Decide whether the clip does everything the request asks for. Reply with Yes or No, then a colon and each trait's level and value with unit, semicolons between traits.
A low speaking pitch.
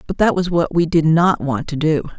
No: medium, 160 Hz